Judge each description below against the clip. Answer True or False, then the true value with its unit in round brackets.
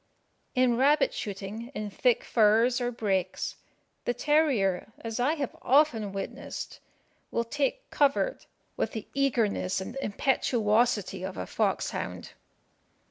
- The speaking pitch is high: True (235 Hz)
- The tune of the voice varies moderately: True (4.6 semitones)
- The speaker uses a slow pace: True (120 wpm)